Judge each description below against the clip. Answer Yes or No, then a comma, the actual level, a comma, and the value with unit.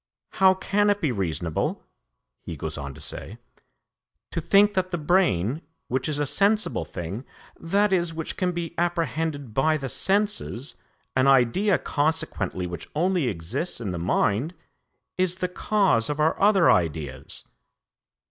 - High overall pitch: No, medium, 155 Hz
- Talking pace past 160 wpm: No, average, 145 wpm